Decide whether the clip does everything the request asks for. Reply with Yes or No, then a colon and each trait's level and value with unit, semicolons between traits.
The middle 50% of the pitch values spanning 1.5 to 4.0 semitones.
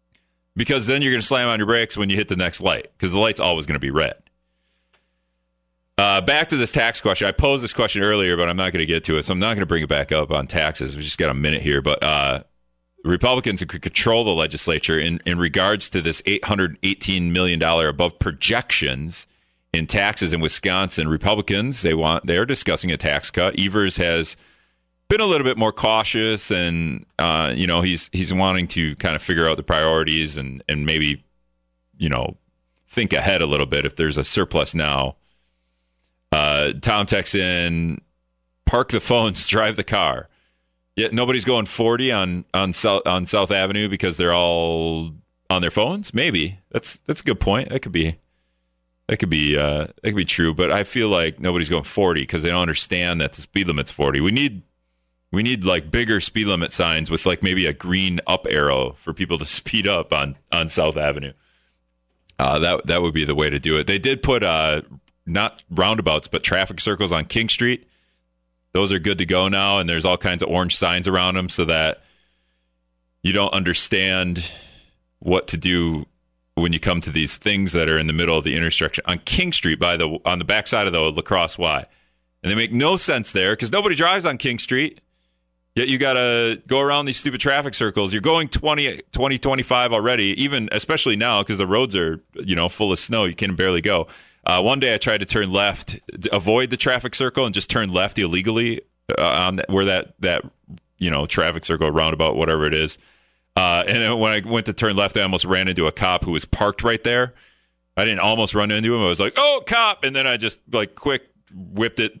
No: wide, 5.5 semitones